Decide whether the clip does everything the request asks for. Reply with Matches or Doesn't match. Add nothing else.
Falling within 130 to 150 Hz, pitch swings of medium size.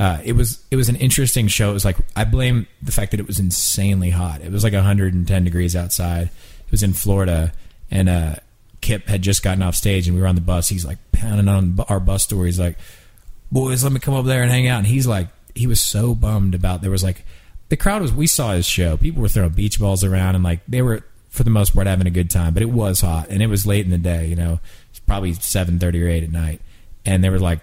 Doesn't match